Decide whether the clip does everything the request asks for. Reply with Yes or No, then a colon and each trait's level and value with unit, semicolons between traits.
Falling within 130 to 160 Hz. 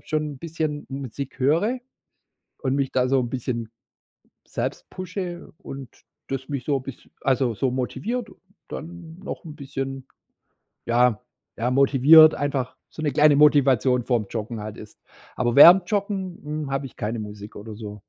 Yes: low, 135 Hz